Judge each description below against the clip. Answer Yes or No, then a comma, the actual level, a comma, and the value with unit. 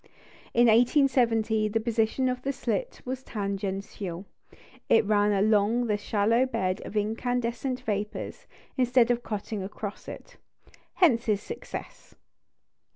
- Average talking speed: No, slow, 120 wpm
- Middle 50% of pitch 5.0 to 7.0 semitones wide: No, average, 3.1 semitones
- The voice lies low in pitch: No, high, 225 Hz